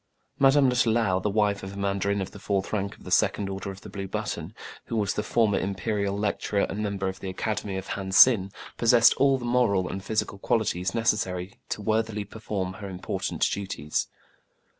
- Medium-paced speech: Yes, average, 195 wpm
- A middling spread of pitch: No, narrow, 2.2 semitones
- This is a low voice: Yes, low, 100 Hz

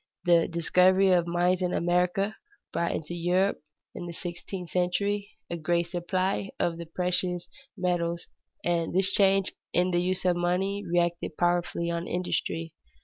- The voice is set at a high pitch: No, medium, 175 Hz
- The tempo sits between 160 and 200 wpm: No, average, 145 wpm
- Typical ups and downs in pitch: No, narrow, 1.3 semitones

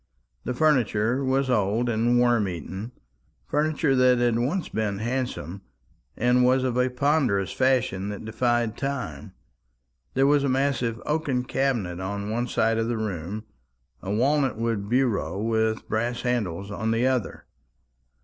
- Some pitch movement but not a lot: Yes, average, 3.4 semitones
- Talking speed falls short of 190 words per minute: Yes, average, 145 wpm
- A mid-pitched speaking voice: No, low, 120 Hz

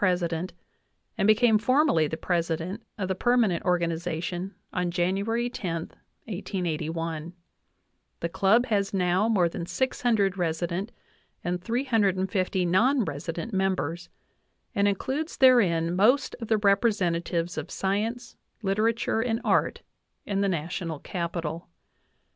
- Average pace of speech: No, slow, 120 wpm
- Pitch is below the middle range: No, high, 190 Hz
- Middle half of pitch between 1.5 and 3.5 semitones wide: No, average, 4.3 semitones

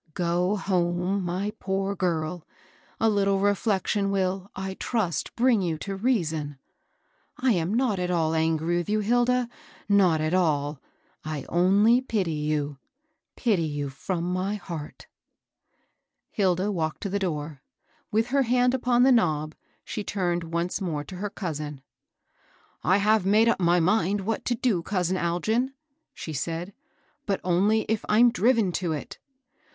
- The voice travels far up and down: No, average, 4.0 semitones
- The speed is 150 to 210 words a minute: Yes, average, 155 wpm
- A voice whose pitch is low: No, medium, 185 Hz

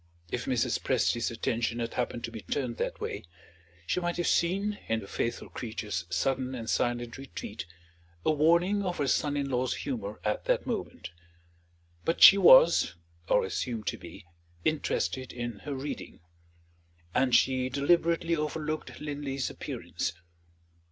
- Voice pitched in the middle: No, low, 130 Hz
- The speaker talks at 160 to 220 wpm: No, average, 145 wpm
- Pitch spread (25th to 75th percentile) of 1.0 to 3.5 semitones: No, average, 4.9 semitones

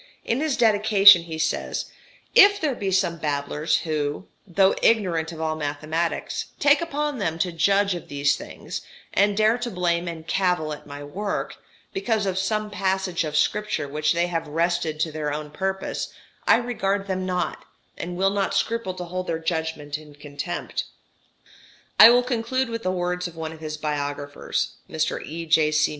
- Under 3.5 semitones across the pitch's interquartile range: No, average, 4.4 semitones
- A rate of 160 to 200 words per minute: Yes, average, 170 wpm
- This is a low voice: No, medium, 175 Hz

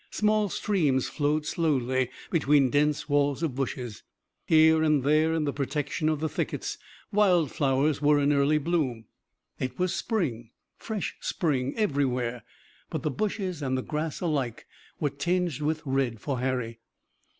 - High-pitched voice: No, medium, 145 Hz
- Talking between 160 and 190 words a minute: No, average, 150 wpm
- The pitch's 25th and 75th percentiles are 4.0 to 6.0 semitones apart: No, average, 3.4 semitones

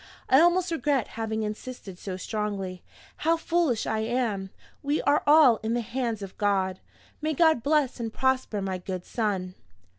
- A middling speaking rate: Yes, average, 160 wpm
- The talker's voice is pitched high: Yes, high, 230 Hz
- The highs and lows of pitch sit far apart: Yes, wide, 6.1 semitones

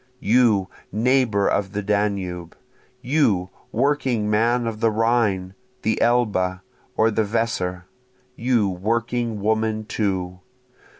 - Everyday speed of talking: No, slow, 110 wpm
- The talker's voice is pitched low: Yes, low, 110 Hz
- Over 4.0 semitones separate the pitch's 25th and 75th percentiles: No, average, 3.2 semitones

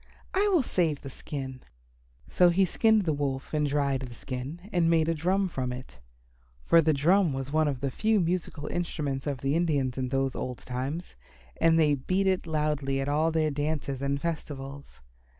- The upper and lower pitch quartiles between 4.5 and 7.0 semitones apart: No, average, 3.7 semitones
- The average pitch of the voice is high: No, medium, 150 Hz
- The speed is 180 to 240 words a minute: Yes, average, 185 wpm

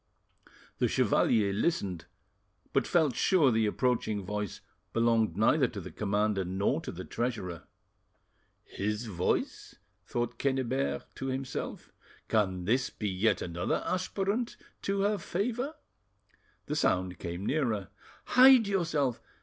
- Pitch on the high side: No, low, 115 Hz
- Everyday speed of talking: No, slow, 120 wpm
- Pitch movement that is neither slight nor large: No, wide, 7.7 semitones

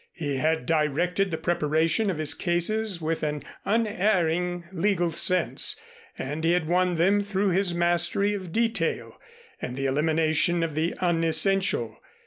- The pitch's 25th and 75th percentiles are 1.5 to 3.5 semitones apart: Yes, average, 3.2 semitones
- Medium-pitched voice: Yes, medium, 175 Hz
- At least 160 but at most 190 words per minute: No, average, 140 wpm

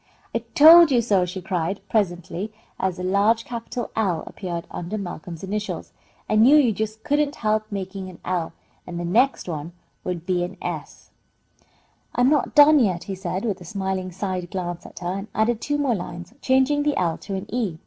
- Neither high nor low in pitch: No, high, 195 Hz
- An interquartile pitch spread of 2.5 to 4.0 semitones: No, average, 4.7 semitones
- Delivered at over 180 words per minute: Yes, average, 190 wpm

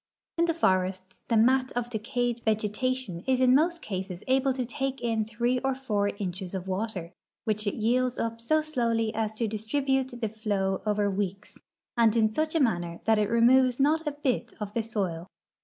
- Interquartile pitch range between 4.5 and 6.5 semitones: No, average, 3.9 semitones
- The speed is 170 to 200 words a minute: Yes, average, 190 wpm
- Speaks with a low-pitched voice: No, high, 225 Hz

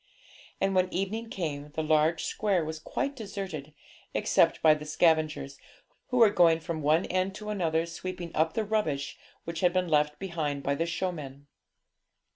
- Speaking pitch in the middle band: Yes, medium, 165 Hz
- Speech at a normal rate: Yes, average, 165 wpm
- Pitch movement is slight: No, average, 3.6 semitones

